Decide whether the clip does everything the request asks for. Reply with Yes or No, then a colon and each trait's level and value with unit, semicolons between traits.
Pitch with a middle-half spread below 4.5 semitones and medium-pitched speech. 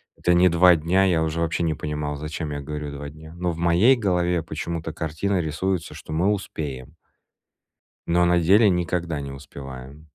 No: average, 2.8 semitones; very low, 80 Hz